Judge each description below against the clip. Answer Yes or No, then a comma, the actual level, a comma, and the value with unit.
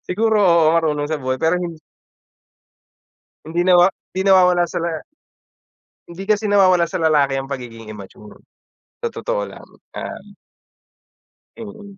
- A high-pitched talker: No, medium, 170 Hz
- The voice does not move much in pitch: No, average, 4.5 semitones